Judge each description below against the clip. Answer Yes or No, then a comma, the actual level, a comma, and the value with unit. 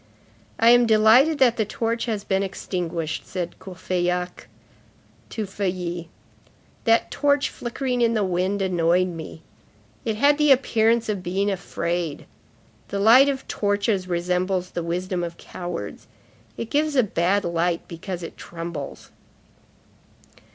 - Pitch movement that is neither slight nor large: Yes, average, 4.6 semitones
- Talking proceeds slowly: Yes, slow, 130 wpm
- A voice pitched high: Yes, high, 195 Hz